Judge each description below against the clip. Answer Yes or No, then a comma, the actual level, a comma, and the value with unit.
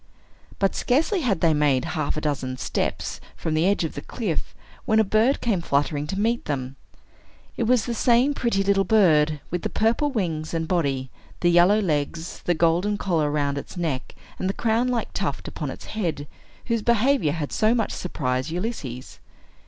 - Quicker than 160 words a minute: Yes, average, 185 wpm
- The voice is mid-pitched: Yes, medium, 175 Hz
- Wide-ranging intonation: Yes, wide, 6.6 semitones